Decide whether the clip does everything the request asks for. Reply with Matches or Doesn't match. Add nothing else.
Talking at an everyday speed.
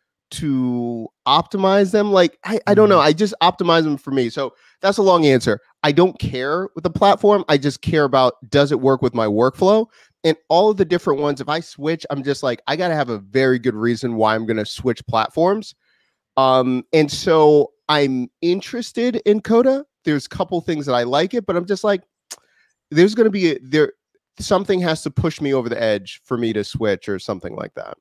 Doesn't match